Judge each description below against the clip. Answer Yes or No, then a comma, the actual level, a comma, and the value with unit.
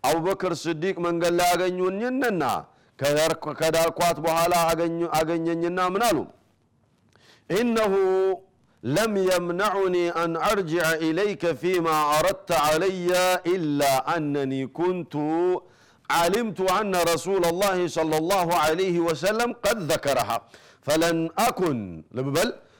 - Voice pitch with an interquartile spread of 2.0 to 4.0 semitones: Yes, narrow, 2.6 semitones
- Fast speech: No, average, 90 wpm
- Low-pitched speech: No, medium, 175 Hz